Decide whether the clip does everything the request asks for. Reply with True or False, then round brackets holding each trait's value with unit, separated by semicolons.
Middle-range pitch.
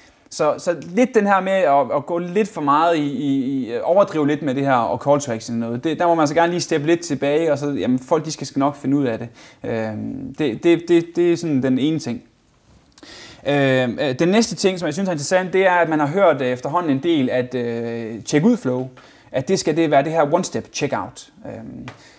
True (150 Hz)